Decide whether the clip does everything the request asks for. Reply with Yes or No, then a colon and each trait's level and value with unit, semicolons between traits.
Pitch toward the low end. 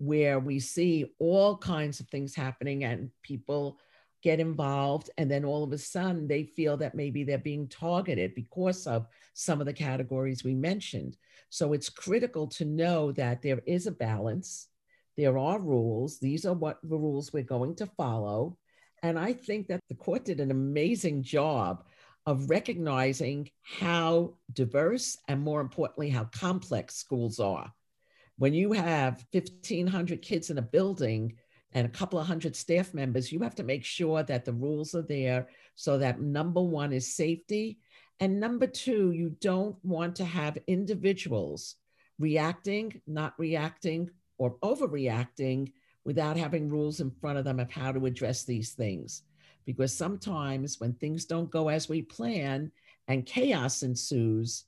No: medium, 150 Hz